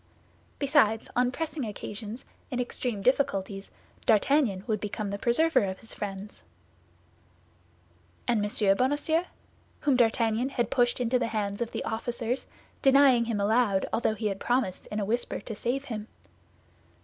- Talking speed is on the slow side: No, average, 145 wpm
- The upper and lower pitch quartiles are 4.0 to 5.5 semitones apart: No, average, 3.4 semitones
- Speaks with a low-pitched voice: No, high, 230 Hz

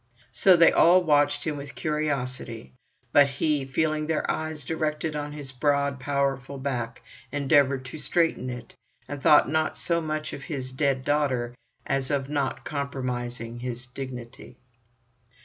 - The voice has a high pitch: No, medium, 140 Hz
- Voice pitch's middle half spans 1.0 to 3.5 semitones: Yes, average, 2.8 semitones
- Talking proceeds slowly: No, average, 145 wpm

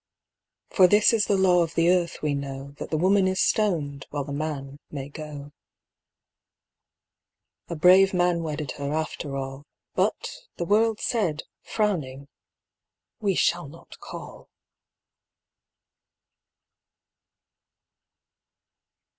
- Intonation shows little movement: No, average, 4.7 semitones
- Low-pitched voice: No, medium, 160 Hz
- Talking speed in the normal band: No, slow, 115 wpm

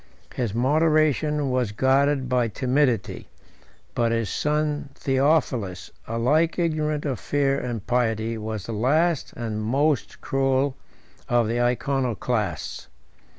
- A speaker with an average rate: No, slow, 110 wpm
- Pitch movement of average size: Yes, average, 4.2 semitones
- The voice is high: No, low, 130 Hz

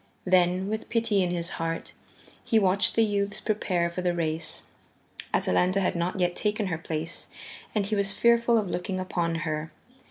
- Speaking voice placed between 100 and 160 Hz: No, medium, 185 Hz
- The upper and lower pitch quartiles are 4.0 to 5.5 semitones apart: No, average, 3.3 semitones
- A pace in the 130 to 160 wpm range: No, average, 170 wpm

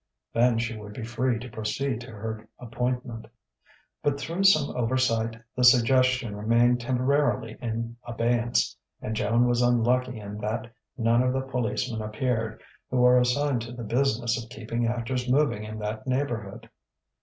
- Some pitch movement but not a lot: No, narrow, 2.1 semitones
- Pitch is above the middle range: No, low, 120 Hz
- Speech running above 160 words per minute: No, average, 155 wpm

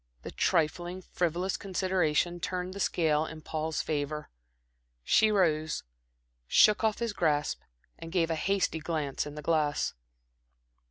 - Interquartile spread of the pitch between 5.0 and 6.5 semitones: No, average, 3.2 semitones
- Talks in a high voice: No, medium, 165 Hz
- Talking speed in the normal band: No, slow, 130 wpm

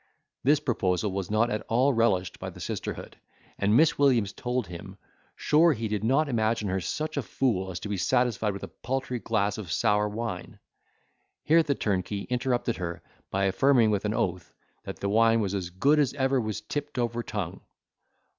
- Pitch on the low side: Yes, low, 110 Hz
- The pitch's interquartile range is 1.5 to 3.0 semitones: No, average, 4.5 semitones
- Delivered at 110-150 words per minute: No, average, 185 wpm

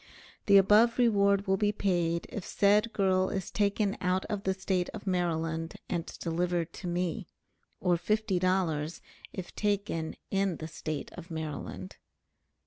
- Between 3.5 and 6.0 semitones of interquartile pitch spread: No, average, 3.0 semitones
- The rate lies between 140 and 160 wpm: Yes, average, 145 wpm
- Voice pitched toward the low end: No, medium, 185 Hz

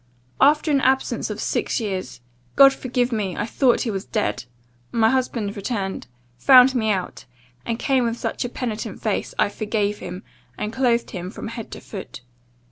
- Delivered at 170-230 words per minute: Yes, average, 175 wpm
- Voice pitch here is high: Yes, high, 230 Hz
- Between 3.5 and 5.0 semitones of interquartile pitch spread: Yes, average, 3.8 semitones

